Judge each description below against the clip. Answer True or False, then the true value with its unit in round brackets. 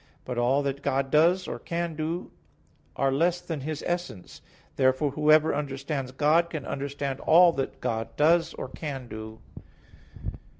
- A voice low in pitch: False (145 Hz)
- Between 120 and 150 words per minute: True (145 wpm)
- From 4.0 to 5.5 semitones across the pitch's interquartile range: False (3.5 semitones)